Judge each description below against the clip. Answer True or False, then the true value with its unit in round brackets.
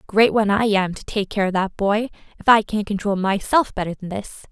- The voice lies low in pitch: False (205 Hz)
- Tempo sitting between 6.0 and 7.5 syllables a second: False (5.5 syllables/s)